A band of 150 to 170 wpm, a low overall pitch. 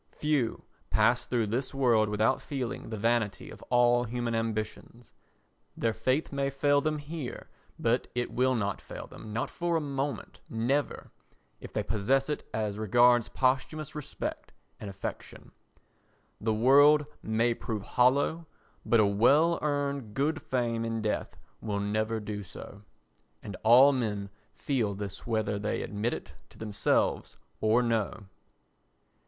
No: average, 140 wpm; low, 120 Hz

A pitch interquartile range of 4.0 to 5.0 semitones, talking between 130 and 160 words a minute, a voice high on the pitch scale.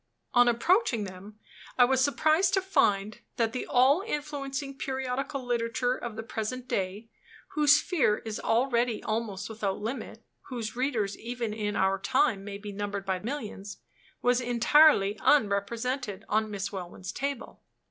Yes: average, 4.3 semitones; average, 145 wpm; high, 235 Hz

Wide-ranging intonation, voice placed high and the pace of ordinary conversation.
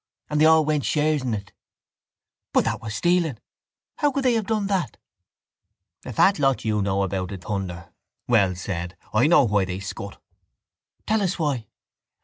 No: wide, 8.7 semitones; low, 120 Hz; average, 170 wpm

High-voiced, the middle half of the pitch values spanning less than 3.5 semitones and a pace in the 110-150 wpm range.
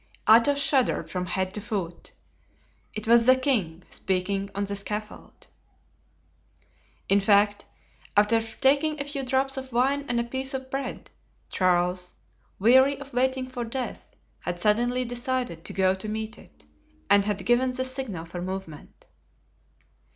No: high, 230 Hz; average, 5.0 semitones; average, 145 wpm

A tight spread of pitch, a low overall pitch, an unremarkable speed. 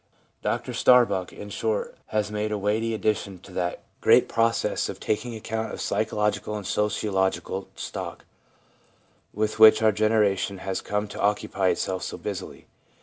Yes: narrow, 1.8 semitones; low, 105 Hz; average, 145 wpm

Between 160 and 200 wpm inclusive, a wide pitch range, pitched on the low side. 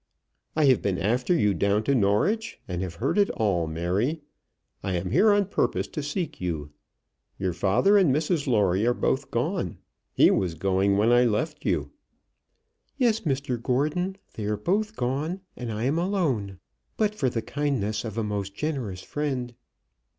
Yes: average, 170 wpm; wide, 7.7 semitones; low, 120 Hz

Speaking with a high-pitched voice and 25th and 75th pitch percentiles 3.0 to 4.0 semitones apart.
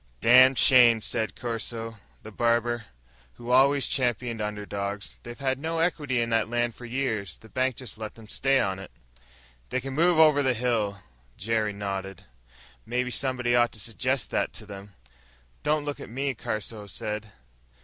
No: low, 120 Hz; average, 3.3 semitones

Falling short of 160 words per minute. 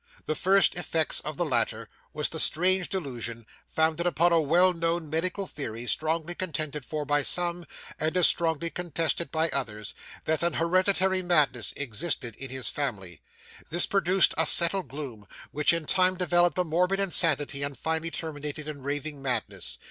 No: average, 165 wpm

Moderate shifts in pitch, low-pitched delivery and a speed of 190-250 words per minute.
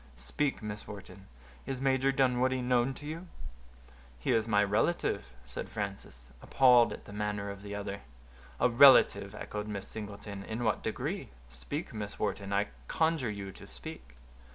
No: average, 4.0 semitones; low, 105 Hz; average, 155 wpm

